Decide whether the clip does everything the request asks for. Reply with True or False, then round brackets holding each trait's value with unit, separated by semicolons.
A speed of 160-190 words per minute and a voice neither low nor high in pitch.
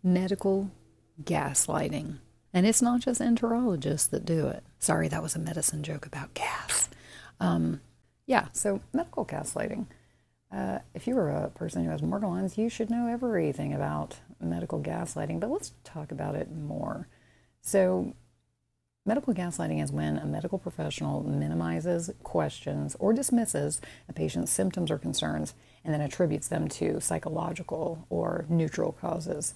False (145 wpm; 155 Hz)